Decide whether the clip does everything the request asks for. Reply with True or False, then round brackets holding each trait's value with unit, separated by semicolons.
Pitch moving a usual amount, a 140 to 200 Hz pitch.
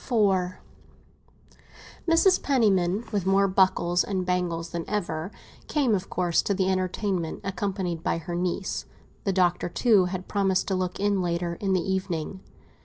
False (2.0 semitones; 185 Hz)